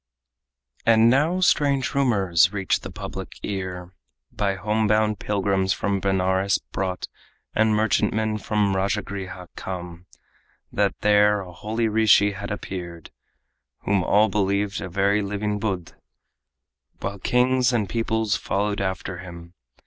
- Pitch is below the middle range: Yes, low, 100 Hz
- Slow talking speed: Yes, slow, 125 wpm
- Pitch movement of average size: No, narrow, 2.3 semitones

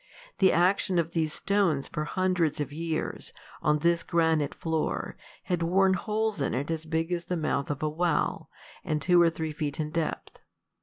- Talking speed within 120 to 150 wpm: No, average, 185 wpm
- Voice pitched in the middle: Yes, medium, 165 Hz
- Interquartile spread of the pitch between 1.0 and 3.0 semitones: Yes, narrow, 2.6 semitones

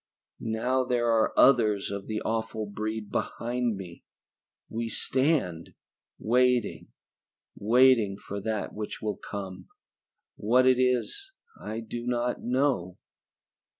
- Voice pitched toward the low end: Yes, low, 115 Hz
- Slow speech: Yes, slow, 115 wpm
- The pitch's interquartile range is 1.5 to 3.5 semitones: Yes, average, 3.1 semitones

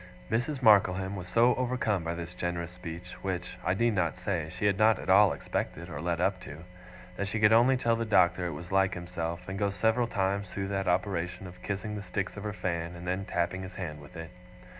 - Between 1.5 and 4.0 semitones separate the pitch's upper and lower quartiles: Yes, average, 2.9 semitones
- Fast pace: Yes, fast, 225 wpm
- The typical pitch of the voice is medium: No, very low, 95 Hz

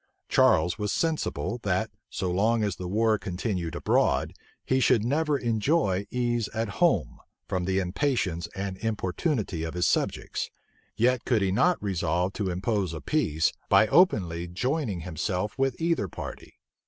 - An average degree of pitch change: Yes, average, 5.0 semitones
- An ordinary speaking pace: Yes, average, 150 wpm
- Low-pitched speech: Yes, low, 100 Hz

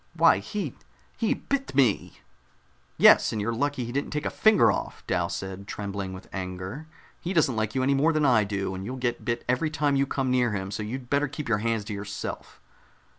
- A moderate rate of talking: No, fast, 215 wpm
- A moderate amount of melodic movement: No, wide, 5.8 semitones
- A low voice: Yes, low, 120 Hz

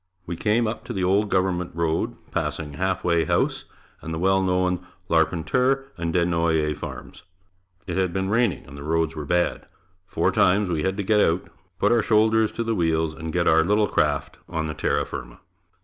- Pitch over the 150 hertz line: No, very low, 90 Hz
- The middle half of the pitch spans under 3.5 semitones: No, average, 3.8 semitones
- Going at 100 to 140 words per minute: No, average, 200 wpm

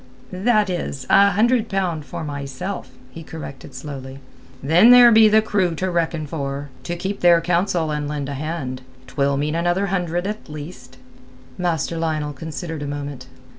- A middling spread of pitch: Yes, average, 4.5 semitones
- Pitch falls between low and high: Yes, medium, 165 Hz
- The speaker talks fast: No, average, 165 wpm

